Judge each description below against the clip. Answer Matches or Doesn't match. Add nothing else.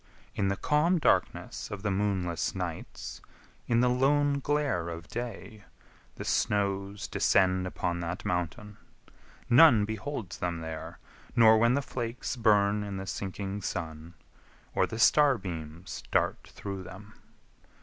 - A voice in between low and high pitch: Doesn't match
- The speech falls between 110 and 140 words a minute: Matches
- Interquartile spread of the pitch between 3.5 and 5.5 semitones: Matches